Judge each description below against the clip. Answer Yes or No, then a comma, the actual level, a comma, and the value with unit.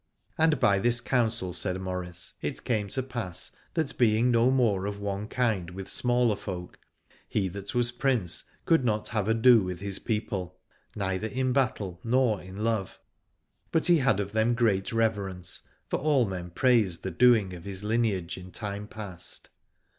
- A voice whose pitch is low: Yes, low, 105 Hz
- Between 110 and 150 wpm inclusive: No, average, 170 wpm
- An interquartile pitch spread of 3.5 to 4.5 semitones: Yes, average, 4.2 semitones